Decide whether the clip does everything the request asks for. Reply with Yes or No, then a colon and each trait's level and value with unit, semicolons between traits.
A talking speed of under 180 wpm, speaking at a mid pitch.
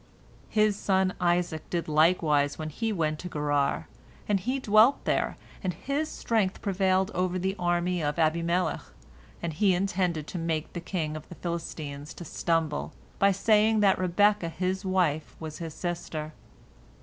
Yes: average, 155 wpm; medium, 175 Hz